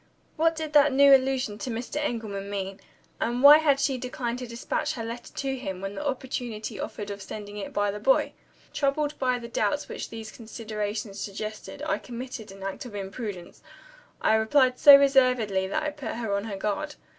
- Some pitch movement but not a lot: Yes, average, 4.7 semitones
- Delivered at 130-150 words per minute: No, average, 190 wpm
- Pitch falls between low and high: No, high, 235 Hz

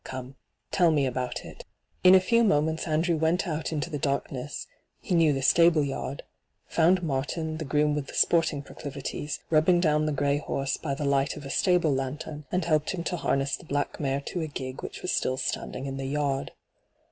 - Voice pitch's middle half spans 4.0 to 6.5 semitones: No, average, 2.9 semitones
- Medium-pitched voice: Yes, medium, 150 Hz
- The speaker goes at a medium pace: No, fast, 215 wpm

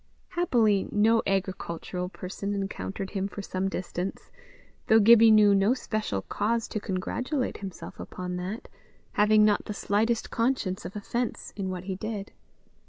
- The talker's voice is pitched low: No, high, 205 Hz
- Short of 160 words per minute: Yes, average, 145 wpm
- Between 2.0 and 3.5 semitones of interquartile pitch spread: Yes, average, 2.7 semitones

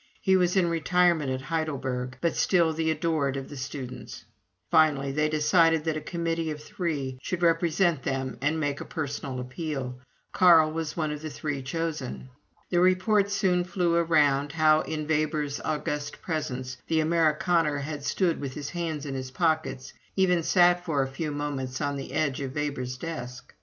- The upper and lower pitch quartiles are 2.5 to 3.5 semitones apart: Yes, average, 3.2 semitones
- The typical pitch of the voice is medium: Yes, medium, 155 Hz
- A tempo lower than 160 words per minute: No, average, 175 wpm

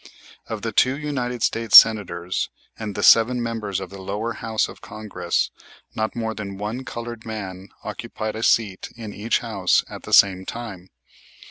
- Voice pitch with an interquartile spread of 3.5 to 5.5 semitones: No, average, 2.8 semitones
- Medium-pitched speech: No, low, 110 Hz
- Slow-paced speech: No, average, 165 wpm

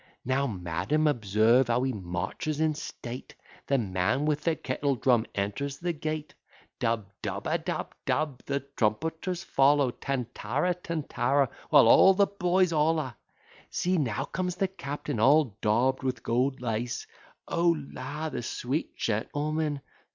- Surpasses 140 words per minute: No, slow, 135 wpm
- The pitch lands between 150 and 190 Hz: No, medium, 140 Hz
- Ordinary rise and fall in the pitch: Yes, average, 4.7 semitones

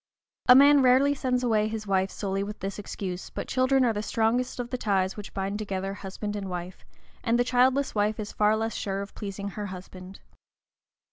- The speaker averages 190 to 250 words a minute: Yes, average, 200 wpm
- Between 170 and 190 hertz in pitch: No, high, 210 Hz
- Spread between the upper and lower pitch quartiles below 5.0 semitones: Yes, average, 4.0 semitones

